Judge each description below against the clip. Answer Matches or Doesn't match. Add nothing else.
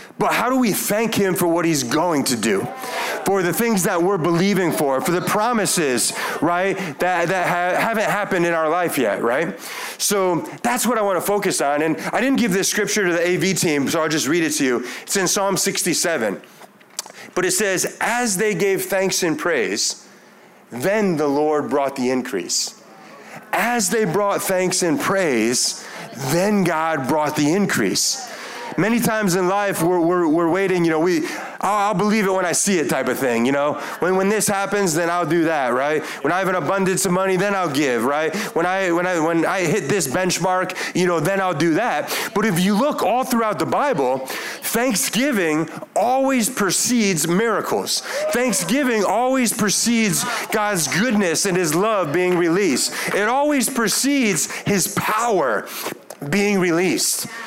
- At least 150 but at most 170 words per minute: Doesn't match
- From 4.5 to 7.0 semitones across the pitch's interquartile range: Doesn't match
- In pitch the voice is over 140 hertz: Matches